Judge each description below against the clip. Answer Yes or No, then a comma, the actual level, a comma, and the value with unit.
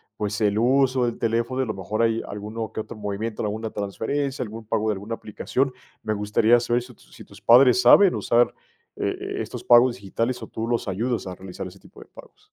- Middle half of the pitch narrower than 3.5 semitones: Yes, average, 2.8 semitones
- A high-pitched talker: No, low, 115 Hz